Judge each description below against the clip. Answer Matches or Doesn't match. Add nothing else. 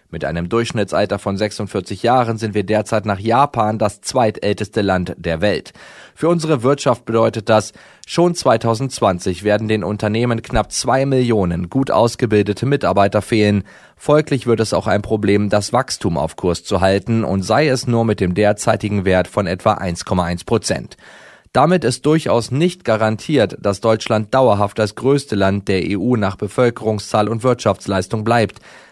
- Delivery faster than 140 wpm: Matches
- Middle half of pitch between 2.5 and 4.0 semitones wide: Matches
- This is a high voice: Doesn't match